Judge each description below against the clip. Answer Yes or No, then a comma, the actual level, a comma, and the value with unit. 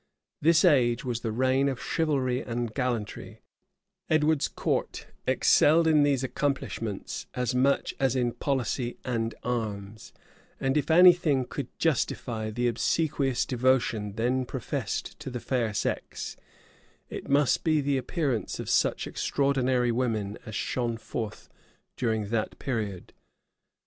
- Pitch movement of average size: Yes, average, 3.3 semitones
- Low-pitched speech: Yes, low, 125 Hz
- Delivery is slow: Yes, slow, 130 wpm